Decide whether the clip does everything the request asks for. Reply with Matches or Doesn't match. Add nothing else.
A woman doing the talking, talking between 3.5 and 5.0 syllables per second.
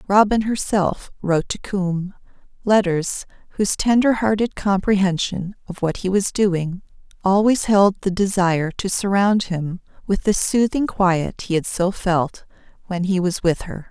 Matches